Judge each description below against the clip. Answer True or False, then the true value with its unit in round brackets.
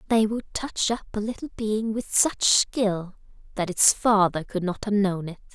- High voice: True (205 Hz)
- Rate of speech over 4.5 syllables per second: False (4.4 syllables/s)